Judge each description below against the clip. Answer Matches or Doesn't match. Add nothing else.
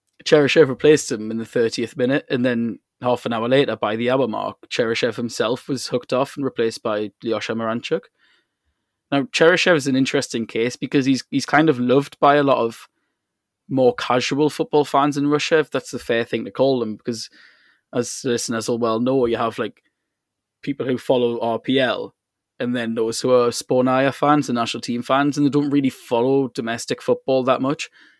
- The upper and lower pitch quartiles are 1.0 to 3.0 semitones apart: Doesn't match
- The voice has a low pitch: Matches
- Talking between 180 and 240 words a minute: Matches